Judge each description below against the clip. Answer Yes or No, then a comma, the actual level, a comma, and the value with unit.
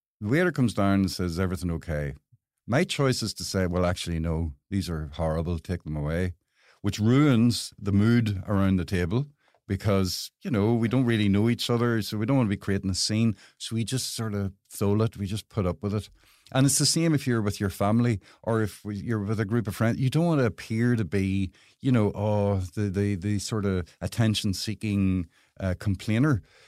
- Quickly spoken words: Yes, fast, 215 wpm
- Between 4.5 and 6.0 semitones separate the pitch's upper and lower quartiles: No, average, 3.7 semitones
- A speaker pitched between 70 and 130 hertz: Yes, low, 105 Hz